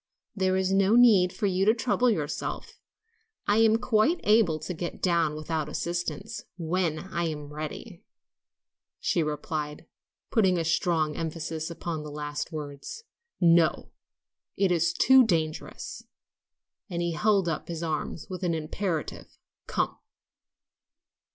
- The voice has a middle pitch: Yes, medium, 170 Hz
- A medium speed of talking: No, slow, 125 wpm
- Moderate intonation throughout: Yes, average, 3.9 semitones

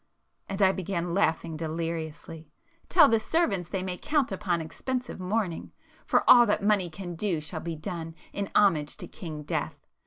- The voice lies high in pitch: No, medium, 180 Hz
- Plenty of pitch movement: No, average, 4.3 semitones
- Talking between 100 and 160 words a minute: Yes, average, 155 wpm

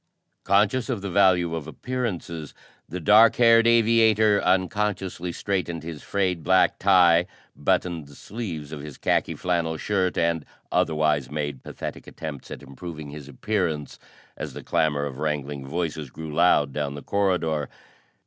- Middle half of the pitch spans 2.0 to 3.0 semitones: No, average, 4.8 semitones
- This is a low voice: Yes, very low, 85 Hz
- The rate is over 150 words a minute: No, average, 145 wpm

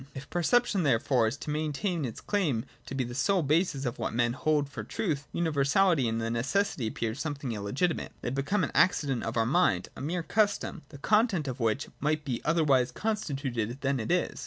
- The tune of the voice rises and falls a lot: Yes, wide, 5.9 semitones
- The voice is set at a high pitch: No, medium, 140 Hz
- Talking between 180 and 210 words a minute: Yes, average, 190 wpm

